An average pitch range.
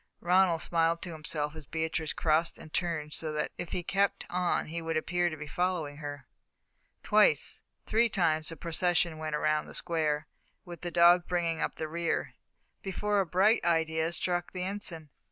No: narrow, 2.2 semitones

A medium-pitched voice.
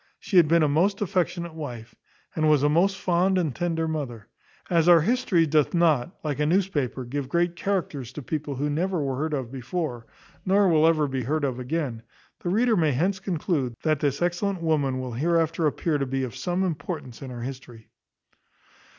Yes: medium, 155 Hz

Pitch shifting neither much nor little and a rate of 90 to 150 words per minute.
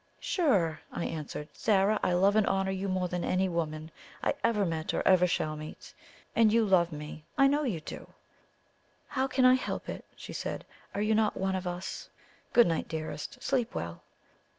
No: average, 4.9 semitones; average, 190 wpm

